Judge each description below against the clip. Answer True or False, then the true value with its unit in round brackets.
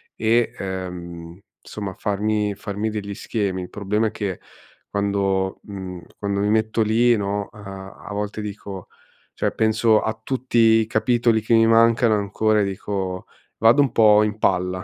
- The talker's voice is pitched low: True (105 Hz)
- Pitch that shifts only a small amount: True (2.2 semitones)